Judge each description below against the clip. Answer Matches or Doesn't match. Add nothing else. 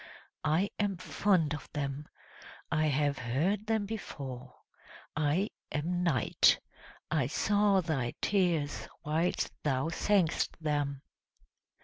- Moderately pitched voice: Matches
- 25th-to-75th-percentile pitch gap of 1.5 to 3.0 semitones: Doesn't match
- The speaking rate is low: Matches